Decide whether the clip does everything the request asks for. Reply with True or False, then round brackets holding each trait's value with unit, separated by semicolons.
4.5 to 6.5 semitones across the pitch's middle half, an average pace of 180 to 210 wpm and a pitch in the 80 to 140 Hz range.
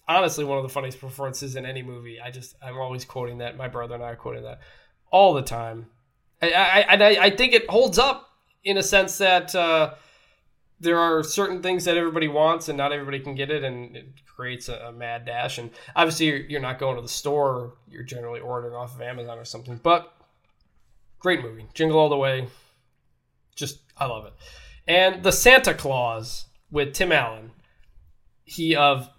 True (5.3 semitones; 195 wpm; 135 Hz)